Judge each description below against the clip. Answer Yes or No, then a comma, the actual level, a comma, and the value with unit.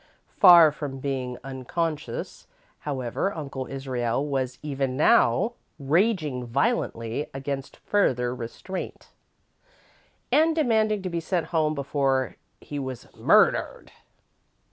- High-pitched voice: No, medium, 140 Hz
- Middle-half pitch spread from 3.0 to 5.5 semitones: Yes, average, 4.5 semitones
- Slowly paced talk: Yes, slow, 100 wpm